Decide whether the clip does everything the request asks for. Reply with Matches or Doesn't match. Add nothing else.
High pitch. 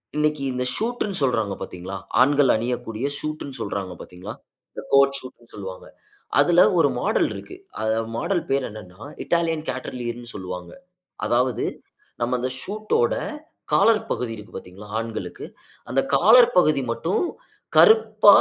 Doesn't match